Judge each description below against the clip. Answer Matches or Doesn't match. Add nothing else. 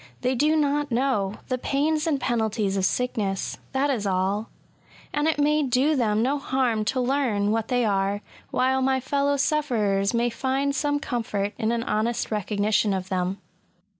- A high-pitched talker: Matches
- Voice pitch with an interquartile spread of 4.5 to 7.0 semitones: Matches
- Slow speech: Doesn't match